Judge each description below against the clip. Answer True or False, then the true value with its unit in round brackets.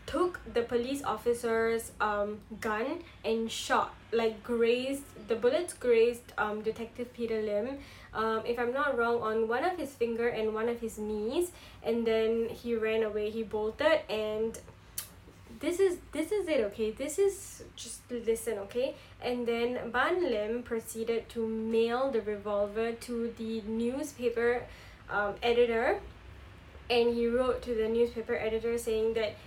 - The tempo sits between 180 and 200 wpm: False (150 wpm)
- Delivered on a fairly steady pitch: True (1.8 semitones)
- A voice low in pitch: False (230 Hz)